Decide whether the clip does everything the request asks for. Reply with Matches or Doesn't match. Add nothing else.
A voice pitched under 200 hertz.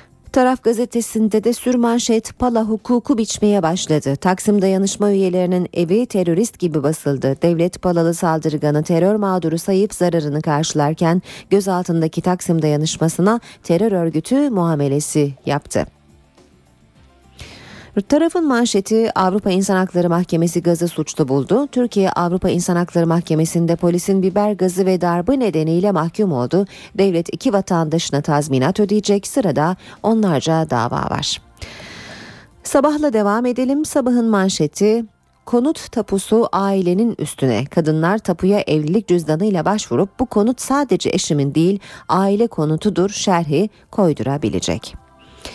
Matches